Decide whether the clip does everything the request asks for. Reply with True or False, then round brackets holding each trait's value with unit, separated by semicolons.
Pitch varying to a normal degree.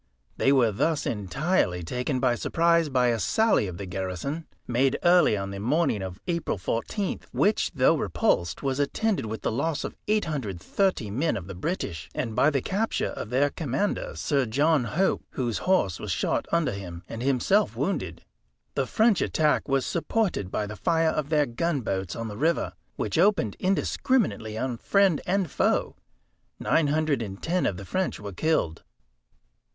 False (8.2 semitones)